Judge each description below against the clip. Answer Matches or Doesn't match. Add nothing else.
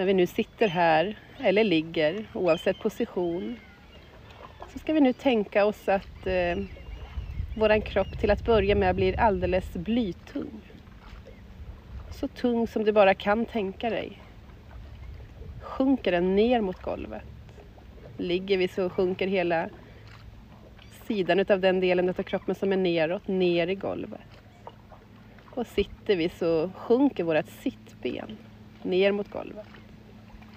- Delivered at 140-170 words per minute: Doesn't match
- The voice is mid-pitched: Matches